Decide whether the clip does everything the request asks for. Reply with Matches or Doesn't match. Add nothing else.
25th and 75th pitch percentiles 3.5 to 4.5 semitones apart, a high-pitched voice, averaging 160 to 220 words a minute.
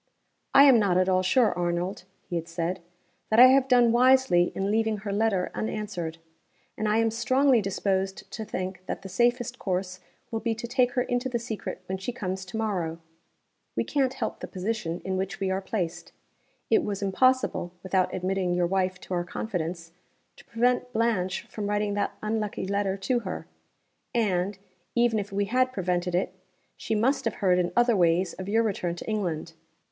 Matches